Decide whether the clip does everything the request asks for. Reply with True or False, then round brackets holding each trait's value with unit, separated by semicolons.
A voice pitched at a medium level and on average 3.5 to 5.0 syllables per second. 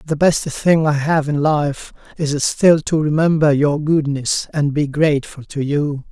True (150 Hz; 4.0 syllables/s)